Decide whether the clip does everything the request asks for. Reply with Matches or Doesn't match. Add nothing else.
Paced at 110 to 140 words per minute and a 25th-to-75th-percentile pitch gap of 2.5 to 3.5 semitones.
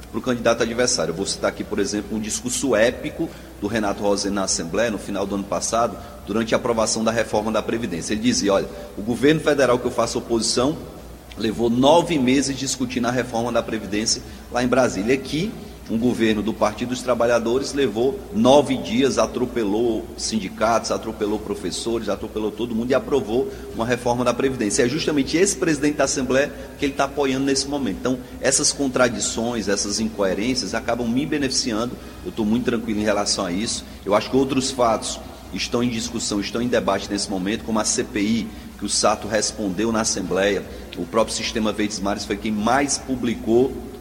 Doesn't match